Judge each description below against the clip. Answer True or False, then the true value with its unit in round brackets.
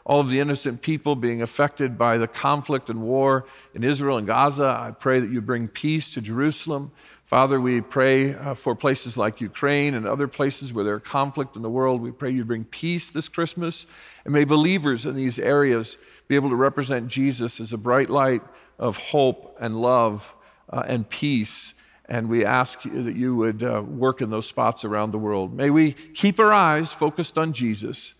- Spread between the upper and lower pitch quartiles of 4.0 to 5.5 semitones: False (3.4 semitones)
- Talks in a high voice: False (130 Hz)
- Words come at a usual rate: True (190 wpm)